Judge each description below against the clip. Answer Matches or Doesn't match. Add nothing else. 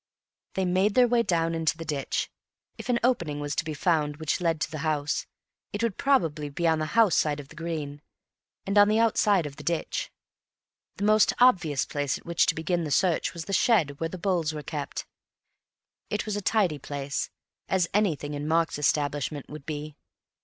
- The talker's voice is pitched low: Doesn't match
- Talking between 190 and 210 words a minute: Matches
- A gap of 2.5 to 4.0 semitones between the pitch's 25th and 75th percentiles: Doesn't match